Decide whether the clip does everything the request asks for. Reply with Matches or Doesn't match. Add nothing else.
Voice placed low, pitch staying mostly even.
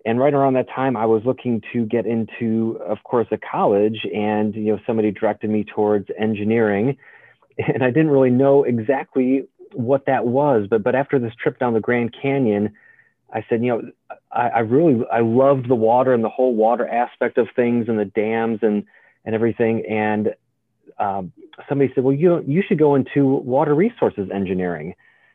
Doesn't match